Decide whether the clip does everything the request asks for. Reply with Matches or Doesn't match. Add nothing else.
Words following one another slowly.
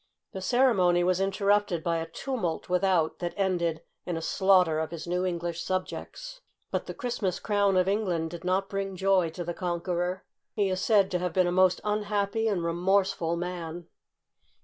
Doesn't match